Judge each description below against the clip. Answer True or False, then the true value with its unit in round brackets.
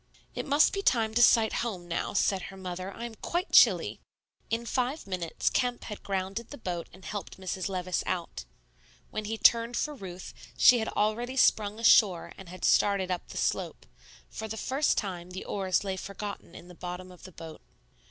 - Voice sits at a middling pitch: False (200 Hz)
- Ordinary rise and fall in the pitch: True (4.0 semitones)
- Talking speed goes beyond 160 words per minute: True (190 wpm)